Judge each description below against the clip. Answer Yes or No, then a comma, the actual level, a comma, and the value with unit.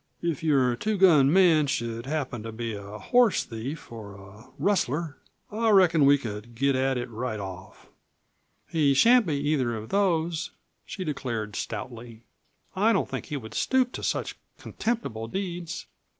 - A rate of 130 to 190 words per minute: Yes, average, 155 wpm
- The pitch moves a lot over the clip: Yes, wide, 7.2 semitones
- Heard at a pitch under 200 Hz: Yes, medium, 140 Hz